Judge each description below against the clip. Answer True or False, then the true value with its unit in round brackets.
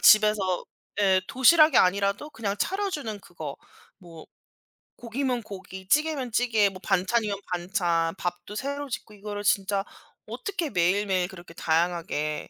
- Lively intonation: False (4.8 semitones)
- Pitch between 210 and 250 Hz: False (200 Hz)